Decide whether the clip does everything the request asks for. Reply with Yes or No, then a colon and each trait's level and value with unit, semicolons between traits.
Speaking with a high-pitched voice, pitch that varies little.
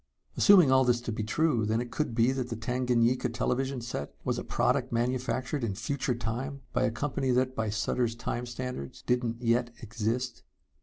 No: low, 120 Hz; narrow, 1.9 semitones